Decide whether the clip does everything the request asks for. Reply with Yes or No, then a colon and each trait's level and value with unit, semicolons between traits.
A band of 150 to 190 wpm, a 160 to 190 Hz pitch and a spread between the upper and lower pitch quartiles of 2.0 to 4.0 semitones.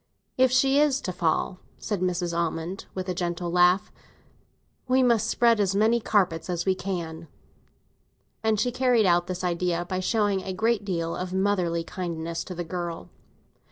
Yes: average, 175 wpm; medium, 185 Hz; average, 3.7 semitones